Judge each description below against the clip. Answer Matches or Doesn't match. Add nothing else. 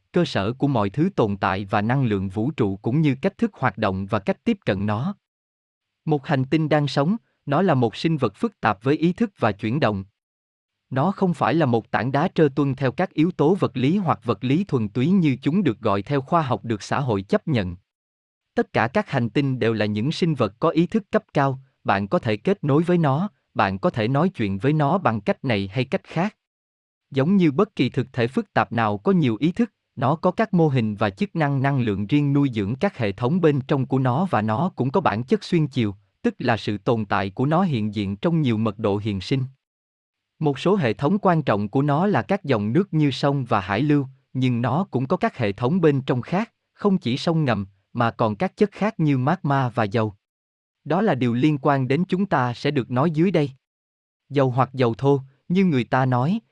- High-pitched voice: Doesn't match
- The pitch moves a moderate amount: Doesn't match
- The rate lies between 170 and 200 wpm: Doesn't match